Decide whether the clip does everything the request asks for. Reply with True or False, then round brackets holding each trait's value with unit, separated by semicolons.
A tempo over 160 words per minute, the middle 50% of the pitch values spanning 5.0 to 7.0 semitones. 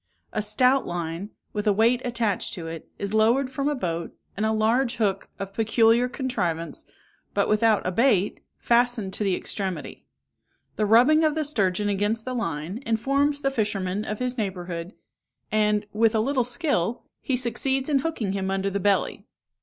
False (170 wpm; 4.3 semitones)